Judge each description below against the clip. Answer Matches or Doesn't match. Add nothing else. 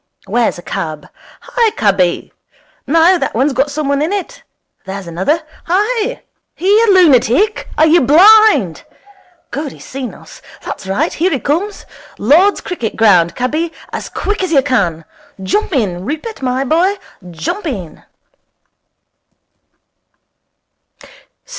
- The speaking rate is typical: Doesn't match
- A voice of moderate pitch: Doesn't match